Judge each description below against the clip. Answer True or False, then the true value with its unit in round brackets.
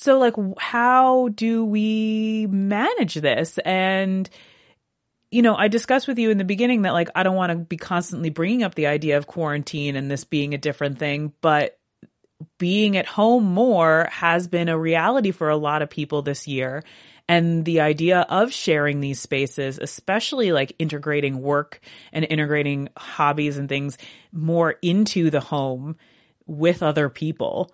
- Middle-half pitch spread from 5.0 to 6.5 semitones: True (5.4 semitones)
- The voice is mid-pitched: True (165 Hz)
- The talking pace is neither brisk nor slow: True (165 wpm)